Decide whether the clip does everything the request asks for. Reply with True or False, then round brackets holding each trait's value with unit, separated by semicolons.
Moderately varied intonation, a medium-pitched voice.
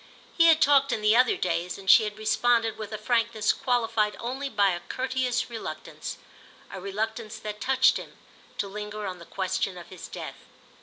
False (3.3 semitones; 215 Hz)